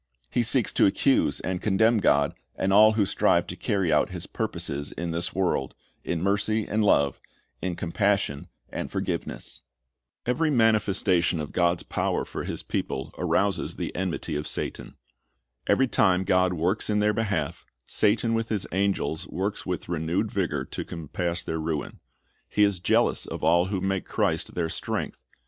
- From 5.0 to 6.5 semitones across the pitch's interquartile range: No, average, 3.8 semitones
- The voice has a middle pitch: No, very low, 95 Hz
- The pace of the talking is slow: No, average, 165 wpm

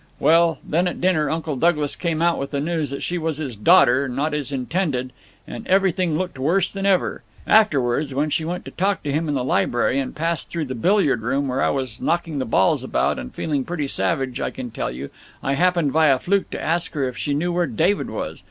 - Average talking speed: No, fast, 230 wpm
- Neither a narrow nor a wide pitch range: Yes, average, 4.3 semitones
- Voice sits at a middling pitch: Yes, medium, 150 Hz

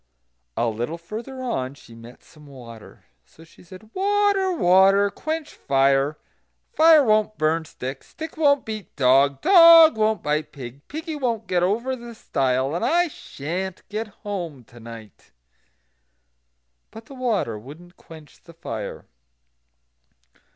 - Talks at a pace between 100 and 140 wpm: Yes, slow, 135 wpm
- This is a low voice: No, medium, 185 Hz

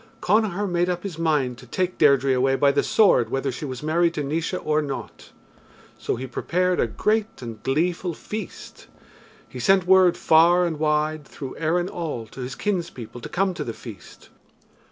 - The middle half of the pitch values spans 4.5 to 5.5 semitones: Yes, average, 5.0 semitones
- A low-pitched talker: No, medium, 160 Hz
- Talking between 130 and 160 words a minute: No, average, 180 wpm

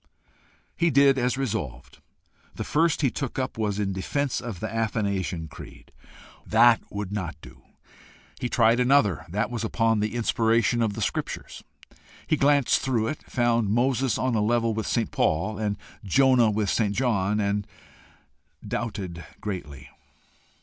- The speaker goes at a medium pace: Yes, average, 150 wpm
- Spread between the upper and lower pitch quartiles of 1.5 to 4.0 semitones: Yes, average, 3.3 semitones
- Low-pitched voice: Yes, low, 115 Hz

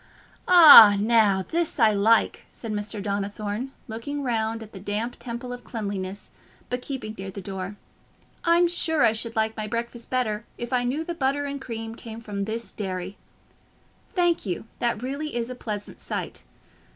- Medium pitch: No, high, 225 Hz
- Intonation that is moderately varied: Yes, average, 3.5 semitones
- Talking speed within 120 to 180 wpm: Yes, average, 170 wpm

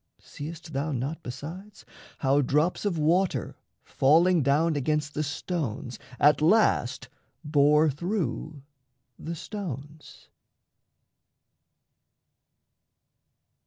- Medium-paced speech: No, slow, 85 wpm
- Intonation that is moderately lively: Yes, average, 3.0 semitones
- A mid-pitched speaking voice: Yes, medium, 150 Hz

